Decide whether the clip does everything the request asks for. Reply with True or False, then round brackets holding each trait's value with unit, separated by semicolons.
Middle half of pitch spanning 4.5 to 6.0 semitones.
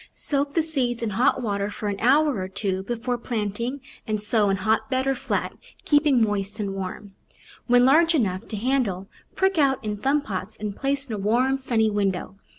True (4.8 semitones)